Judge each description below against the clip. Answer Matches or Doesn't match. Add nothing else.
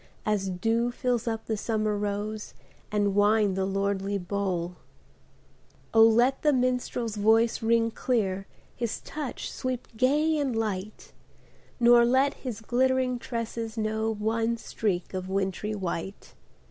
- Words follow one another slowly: Matches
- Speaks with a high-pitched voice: Matches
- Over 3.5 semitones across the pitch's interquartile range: Doesn't match